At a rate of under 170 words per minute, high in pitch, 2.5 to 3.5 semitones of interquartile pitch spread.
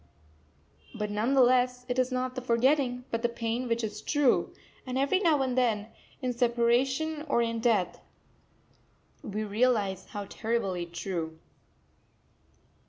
Yes: average, 140 wpm; high, 240 Hz; average, 3.0 semitones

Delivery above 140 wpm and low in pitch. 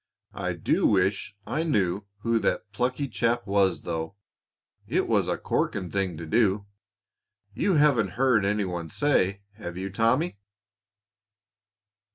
No: slow, 135 wpm; low, 100 Hz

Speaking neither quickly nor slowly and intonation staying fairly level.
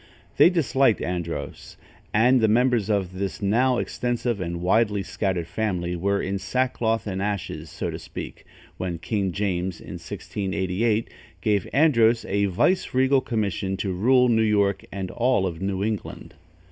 No: average, 145 wpm; average, 3.8 semitones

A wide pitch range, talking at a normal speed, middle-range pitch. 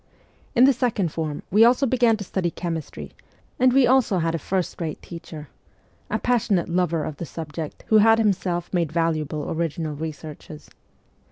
Yes: wide, 5.7 semitones; average, 165 wpm; medium, 170 Hz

